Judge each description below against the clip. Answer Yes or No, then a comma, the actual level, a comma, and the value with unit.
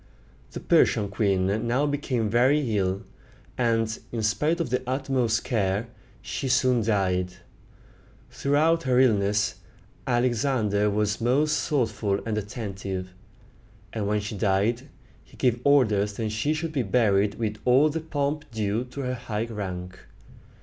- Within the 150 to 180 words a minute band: No, slow, 135 wpm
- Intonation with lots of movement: No, average, 4.1 semitones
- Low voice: Yes, low, 115 Hz